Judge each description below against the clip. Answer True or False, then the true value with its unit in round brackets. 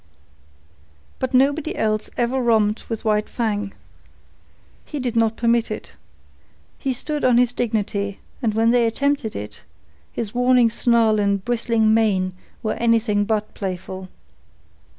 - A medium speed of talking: False (130 wpm)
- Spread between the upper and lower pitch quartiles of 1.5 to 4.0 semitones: True (2.6 semitones)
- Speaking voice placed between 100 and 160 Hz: False (225 Hz)